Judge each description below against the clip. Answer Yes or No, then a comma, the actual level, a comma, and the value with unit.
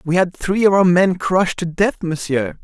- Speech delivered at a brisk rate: Yes, fast, 225 wpm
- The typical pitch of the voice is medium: Yes, medium, 175 Hz